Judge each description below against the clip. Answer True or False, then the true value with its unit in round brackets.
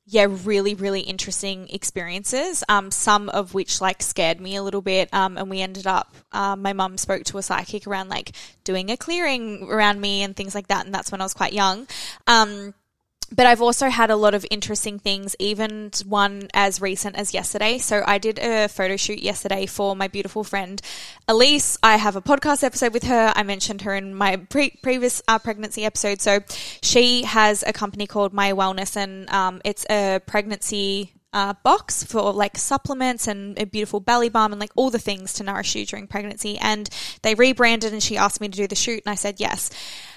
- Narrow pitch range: True (1.8 semitones)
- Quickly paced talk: True (210 wpm)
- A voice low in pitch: False (205 Hz)